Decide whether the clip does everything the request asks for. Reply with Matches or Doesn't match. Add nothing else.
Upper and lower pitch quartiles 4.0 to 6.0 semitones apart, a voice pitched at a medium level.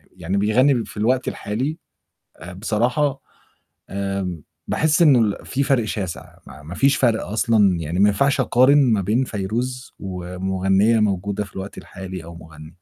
Doesn't match